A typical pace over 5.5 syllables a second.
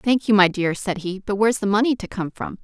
Yes: 5.9 syllables/s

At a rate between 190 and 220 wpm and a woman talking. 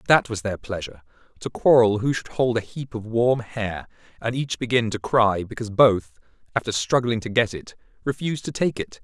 No: average, 200 wpm; male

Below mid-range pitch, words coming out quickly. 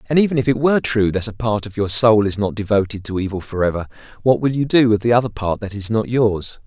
Yes: low, 110 Hz; fast, 270 wpm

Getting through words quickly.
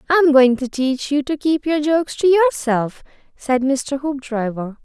No: average, 175 wpm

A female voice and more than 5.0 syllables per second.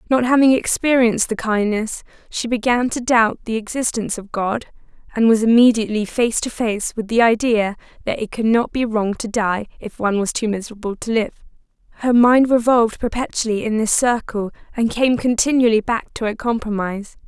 Yes: female; 5.5 syllables/s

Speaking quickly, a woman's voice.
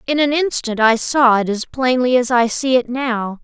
Yes: fast, 225 wpm; female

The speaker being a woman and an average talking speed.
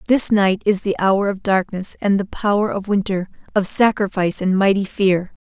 Yes: female; average, 190 wpm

